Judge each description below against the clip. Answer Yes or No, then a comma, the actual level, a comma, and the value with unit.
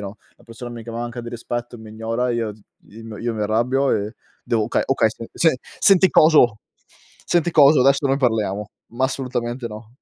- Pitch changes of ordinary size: Yes, average, 3.0 semitones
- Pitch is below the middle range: Yes, low, 120 Hz